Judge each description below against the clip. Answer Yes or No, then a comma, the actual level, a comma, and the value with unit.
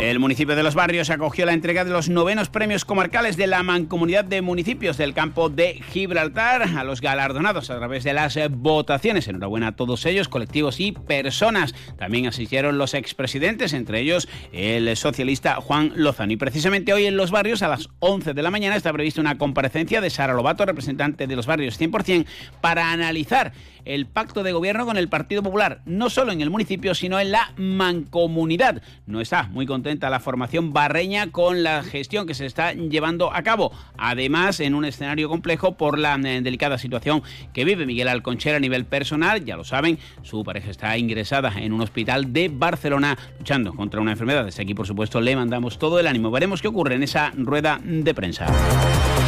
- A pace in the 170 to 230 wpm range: Yes, fast, 190 wpm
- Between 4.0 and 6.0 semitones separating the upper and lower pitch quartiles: Yes, average, 4.9 semitones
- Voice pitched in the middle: Yes, medium, 150 Hz